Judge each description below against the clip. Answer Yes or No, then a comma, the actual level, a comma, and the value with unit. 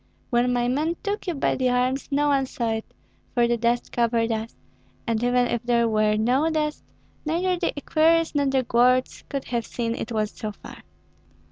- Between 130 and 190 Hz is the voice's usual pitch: No, high, 245 Hz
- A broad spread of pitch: No, average, 3.6 semitones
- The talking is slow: No, average, 195 wpm